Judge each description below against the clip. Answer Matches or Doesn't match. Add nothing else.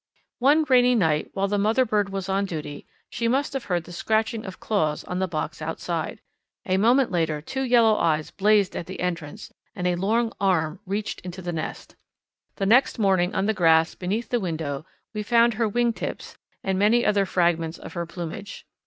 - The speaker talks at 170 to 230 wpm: Matches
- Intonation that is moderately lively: Matches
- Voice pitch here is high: Matches